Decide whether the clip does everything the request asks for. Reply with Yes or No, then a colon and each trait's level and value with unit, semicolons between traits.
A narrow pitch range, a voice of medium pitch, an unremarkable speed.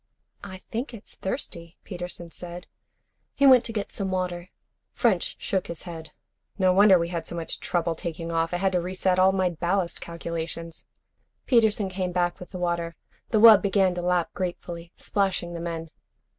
Yes: narrow, 2.1 semitones; medium, 180 Hz; average, 175 wpm